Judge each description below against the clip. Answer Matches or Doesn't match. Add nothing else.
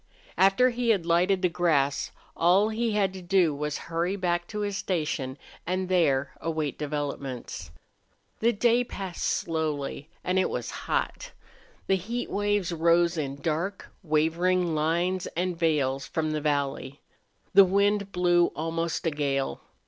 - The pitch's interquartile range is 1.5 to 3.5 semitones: Doesn't match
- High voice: Doesn't match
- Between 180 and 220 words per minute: Doesn't match